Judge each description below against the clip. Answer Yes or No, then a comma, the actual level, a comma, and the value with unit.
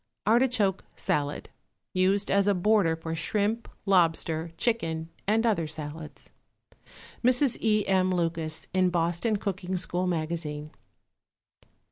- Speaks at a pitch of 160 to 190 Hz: Yes, medium, 185 Hz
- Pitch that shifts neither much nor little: Yes, average, 4.2 semitones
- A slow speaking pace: Yes, slow, 110 wpm